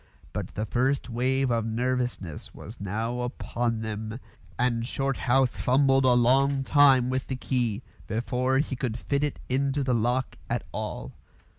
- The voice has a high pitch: No, low, 125 Hz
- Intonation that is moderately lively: No, narrow, 2.3 semitones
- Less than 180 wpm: Yes, average, 150 wpm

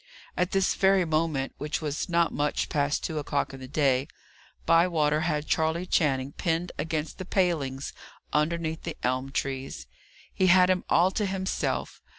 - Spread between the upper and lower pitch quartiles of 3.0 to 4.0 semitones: Yes, average, 3.7 semitones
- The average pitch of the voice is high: No, medium, 160 Hz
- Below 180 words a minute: Yes, average, 160 wpm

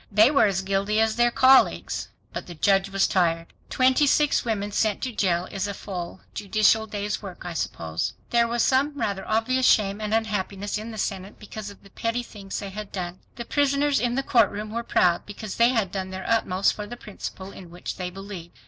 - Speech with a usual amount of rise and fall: Yes, average, 3.2 semitones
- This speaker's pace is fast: Yes, fast, 210 wpm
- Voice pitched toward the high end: Yes, high, 205 Hz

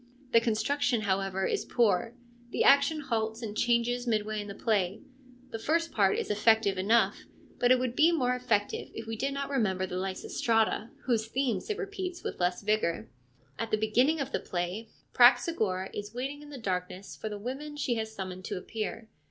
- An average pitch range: Yes, average, 4.0 semitones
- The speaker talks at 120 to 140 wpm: No, average, 185 wpm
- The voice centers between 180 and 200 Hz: No, high, 225 Hz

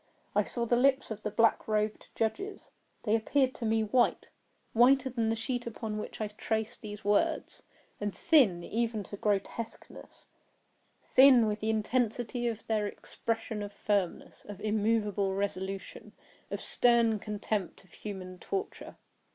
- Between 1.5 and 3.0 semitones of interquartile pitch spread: Yes, narrow, 2.4 semitones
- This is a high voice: Yes, high, 220 Hz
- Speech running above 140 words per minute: No, slow, 135 wpm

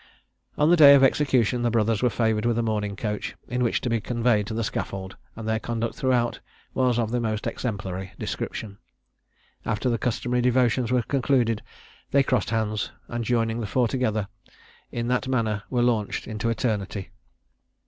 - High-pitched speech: No, low, 115 Hz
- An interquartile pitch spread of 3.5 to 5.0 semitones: No, narrow, 2.4 semitones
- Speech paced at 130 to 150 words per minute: No, average, 175 wpm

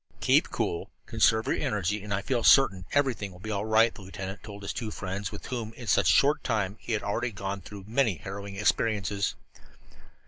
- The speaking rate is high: Yes, fast, 210 wpm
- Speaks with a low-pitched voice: Yes, low, 105 Hz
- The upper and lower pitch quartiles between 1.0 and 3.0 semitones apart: Yes, narrow, 2.5 semitones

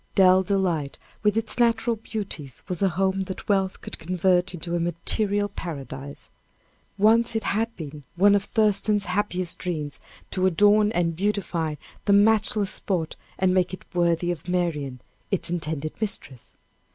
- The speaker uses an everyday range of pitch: Yes, average, 3.3 semitones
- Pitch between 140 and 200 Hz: Yes, medium, 185 Hz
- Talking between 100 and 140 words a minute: No, average, 150 wpm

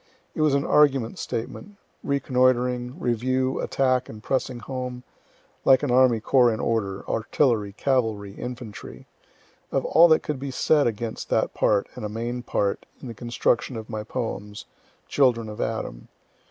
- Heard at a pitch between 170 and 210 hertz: No, low, 125 Hz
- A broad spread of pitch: No, average, 2.9 semitones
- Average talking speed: Yes, average, 155 wpm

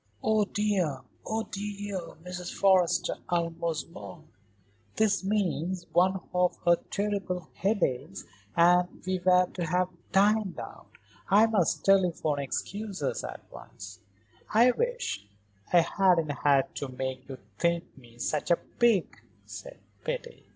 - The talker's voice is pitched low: No, medium, 180 Hz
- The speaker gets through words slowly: Yes, slow, 125 wpm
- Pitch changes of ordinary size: Yes, average, 3.9 semitones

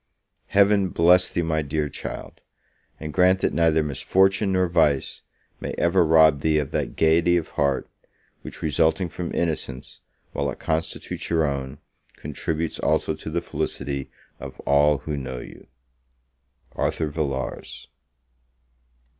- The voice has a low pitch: Yes, very low, 80 Hz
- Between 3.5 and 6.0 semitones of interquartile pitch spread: No, average, 3.0 semitones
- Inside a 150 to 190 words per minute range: No, slow, 135 wpm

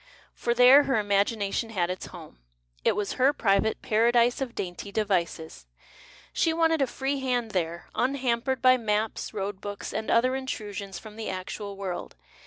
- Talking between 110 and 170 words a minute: Yes, average, 160 wpm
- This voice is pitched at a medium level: No, high, 220 Hz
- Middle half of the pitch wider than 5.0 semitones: No, average, 4.4 semitones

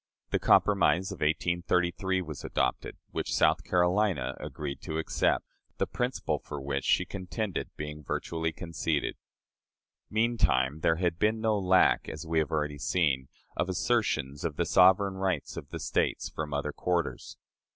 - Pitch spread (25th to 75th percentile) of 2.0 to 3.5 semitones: No, average, 3.9 semitones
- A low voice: Yes, very low, 85 Hz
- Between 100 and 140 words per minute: No, average, 150 wpm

